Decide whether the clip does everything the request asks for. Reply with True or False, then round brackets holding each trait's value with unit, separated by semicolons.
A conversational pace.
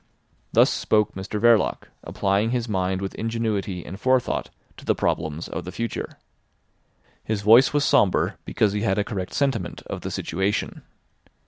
True (155 wpm)